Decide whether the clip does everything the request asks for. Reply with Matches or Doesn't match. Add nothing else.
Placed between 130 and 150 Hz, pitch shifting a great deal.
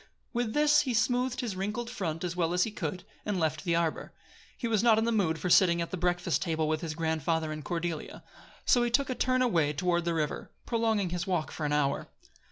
Doesn't match